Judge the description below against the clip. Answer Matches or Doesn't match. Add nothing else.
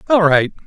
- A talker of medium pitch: Matches